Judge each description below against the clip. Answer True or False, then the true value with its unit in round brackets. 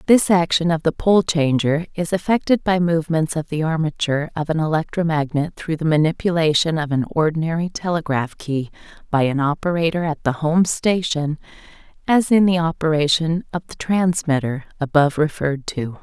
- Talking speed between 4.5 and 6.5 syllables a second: True (5.3 syllables/s)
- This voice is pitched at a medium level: True (160 Hz)